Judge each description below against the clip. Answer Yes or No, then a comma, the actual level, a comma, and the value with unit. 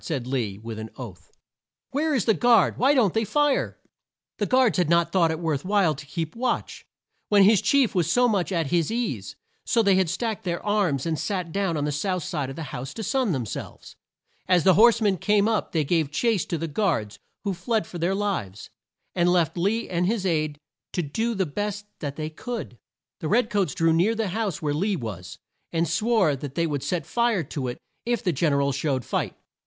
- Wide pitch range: Yes, wide, 5.9 semitones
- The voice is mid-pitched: Yes, medium, 175 Hz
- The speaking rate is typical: No, fast, 220 wpm